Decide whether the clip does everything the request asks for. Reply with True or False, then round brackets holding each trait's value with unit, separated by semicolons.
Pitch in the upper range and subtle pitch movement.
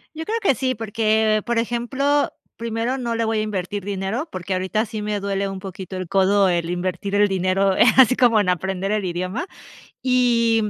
False (210 Hz; 3.5 semitones)